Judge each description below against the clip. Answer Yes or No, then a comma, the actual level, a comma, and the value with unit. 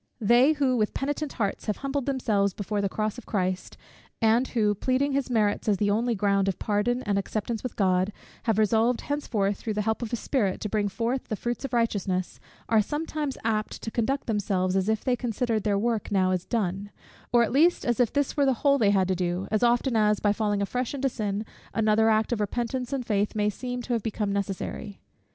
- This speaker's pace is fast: Yes, fast, 220 wpm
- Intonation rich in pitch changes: No, average, 3.4 semitones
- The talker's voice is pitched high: Yes, high, 220 Hz